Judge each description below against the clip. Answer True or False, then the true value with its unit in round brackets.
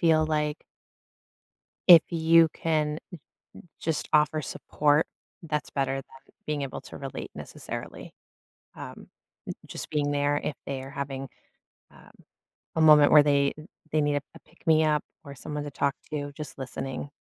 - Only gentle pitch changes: True (1.7 semitones)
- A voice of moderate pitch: True (150 Hz)